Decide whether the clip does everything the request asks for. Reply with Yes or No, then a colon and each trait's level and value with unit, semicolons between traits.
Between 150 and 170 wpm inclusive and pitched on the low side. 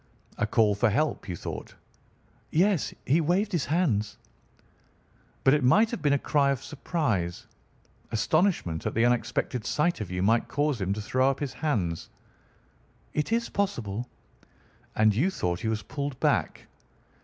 Yes: average, 155 wpm; low, 130 Hz